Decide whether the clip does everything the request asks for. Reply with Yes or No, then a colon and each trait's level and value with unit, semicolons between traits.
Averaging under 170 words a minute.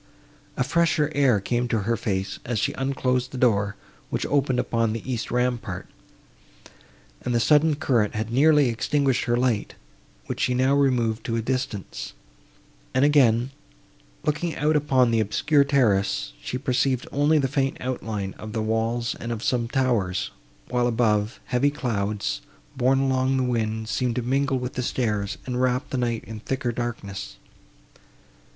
Yes: average, 160 wpm